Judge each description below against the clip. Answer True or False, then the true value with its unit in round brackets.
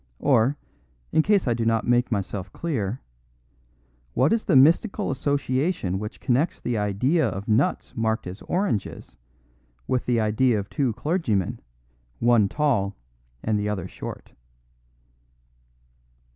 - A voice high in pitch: False (120 Hz)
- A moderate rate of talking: False (130 wpm)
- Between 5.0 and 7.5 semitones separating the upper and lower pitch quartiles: True (5.5 semitones)